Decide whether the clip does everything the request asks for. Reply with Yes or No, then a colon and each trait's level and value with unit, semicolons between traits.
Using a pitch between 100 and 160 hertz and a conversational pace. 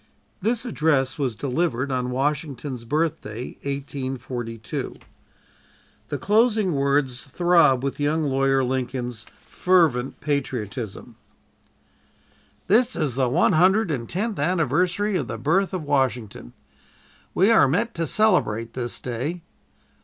No: medium, 140 Hz; slow, 115 wpm